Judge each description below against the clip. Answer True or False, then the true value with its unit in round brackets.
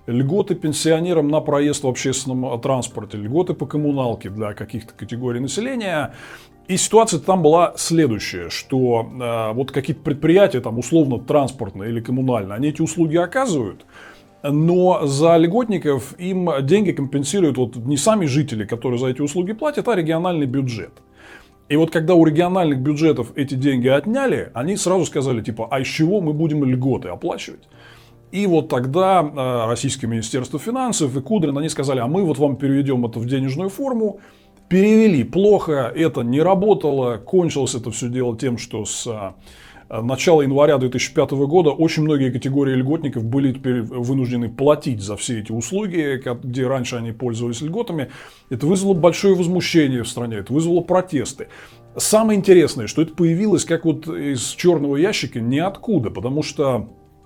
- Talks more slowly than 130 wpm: False (150 wpm)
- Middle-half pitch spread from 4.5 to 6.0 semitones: True (5.3 semitones)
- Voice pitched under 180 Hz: True (140 Hz)